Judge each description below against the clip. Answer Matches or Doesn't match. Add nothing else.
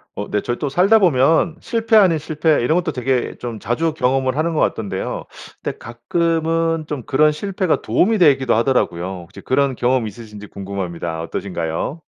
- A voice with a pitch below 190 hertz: Matches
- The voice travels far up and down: Matches